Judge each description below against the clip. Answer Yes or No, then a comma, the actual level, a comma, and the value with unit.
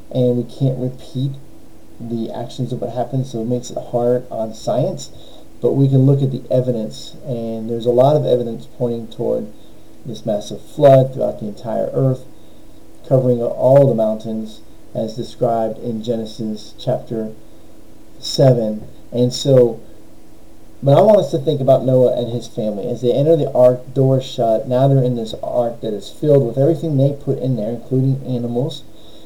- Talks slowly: No, average, 170 wpm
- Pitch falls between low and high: No, low, 125 Hz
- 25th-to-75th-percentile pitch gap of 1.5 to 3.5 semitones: Yes, narrow, 2.6 semitones